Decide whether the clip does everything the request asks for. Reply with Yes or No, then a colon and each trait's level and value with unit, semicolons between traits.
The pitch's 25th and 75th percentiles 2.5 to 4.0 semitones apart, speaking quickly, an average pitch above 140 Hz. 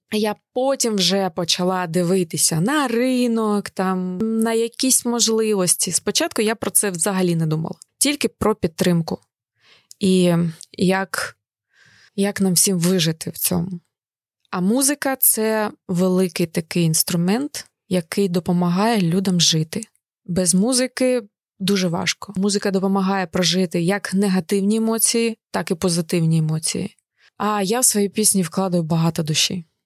No: average, 3.5 semitones; average, 125 wpm; high, 190 Hz